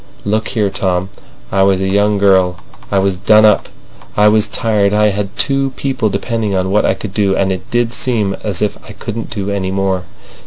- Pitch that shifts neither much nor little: No, narrow, 1.9 semitones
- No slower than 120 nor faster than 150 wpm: No, fast, 205 wpm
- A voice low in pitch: Yes, low, 100 Hz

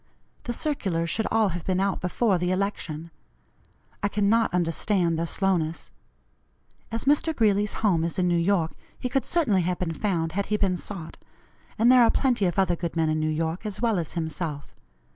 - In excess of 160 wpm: Yes, average, 190 wpm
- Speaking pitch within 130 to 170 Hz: No, medium, 185 Hz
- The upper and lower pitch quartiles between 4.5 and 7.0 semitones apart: No, average, 4.1 semitones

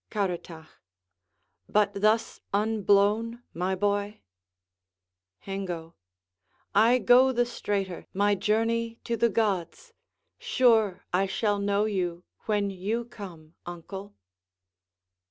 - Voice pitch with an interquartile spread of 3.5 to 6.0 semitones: No, average, 2.9 semitones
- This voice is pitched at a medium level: No, high, 205 Hz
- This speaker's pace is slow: Yes, slow, 100 wpm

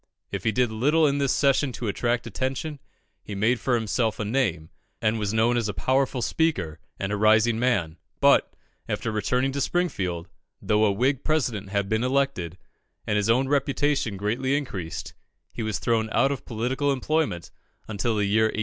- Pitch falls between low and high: No, low, 115 Hz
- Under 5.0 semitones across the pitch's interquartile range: Yes, average, 4.4 semitones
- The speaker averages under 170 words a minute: No, average, 180 wpm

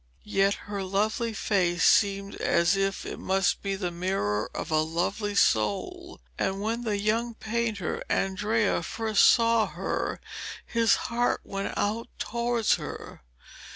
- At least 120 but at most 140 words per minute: Yes, slow, 135 wpm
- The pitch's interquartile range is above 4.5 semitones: No, average, 2.9 semitones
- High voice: Yes, high, 200 Hz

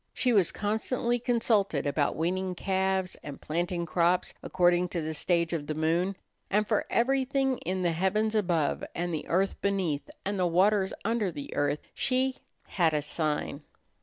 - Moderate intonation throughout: Yes, average, 4.1 semitones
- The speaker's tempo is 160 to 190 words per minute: Yes, average, 165 wpm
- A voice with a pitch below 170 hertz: No, medium, 185 Hz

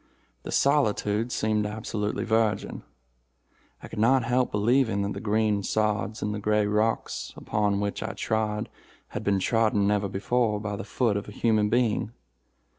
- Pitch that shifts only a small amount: Yes, narrow, 1.6 semitones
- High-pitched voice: No, low, 105 Hz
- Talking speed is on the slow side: No, average, 160 wpm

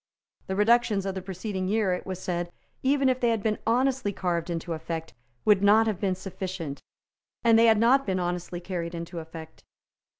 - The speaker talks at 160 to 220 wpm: Yes, average, 190 wpm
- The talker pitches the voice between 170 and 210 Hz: Yes, high, 190 Hz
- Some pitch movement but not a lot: Yes, average, 4.3 semitones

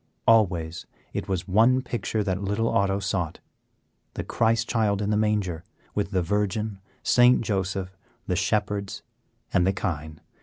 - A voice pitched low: Yes, low, 100 Hz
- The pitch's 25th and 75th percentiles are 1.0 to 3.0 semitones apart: Yes, average, 2.7 semitones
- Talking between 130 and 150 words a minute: Yes, average, 145 wpm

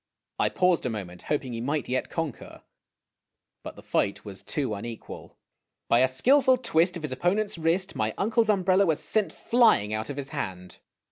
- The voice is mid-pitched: Yes, medium, 150 Hz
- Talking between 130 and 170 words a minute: No, average, 180 wpm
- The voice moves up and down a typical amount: No, wide, 8.7 semitones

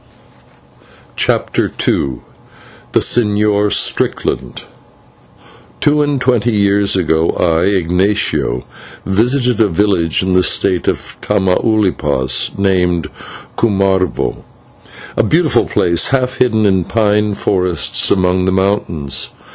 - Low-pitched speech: Yes, low, 100 Hz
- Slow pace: Yes, slow, 100 wpm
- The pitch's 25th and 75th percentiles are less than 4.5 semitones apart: Yes, average, 3.0 semitones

